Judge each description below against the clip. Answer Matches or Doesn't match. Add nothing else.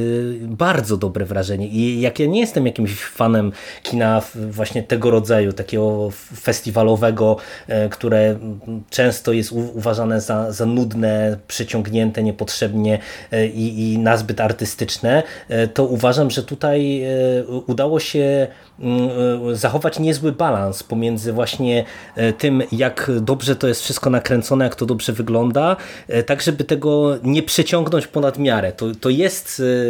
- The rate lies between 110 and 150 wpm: Matches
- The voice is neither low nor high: Doesn't match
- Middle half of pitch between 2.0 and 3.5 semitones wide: Matches